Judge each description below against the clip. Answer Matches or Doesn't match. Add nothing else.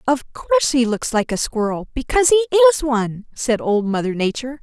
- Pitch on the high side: Matches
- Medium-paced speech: Matches